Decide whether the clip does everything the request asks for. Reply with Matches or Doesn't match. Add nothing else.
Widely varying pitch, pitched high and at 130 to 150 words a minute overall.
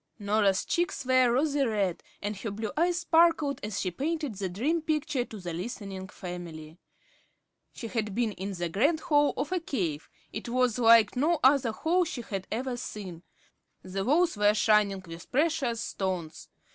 Doesn't match